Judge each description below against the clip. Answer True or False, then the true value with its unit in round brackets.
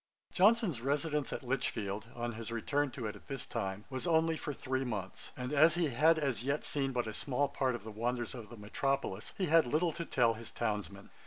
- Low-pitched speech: True (130 Hz)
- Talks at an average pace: False (220 wpm)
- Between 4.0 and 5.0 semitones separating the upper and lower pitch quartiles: True (4.6 semitones)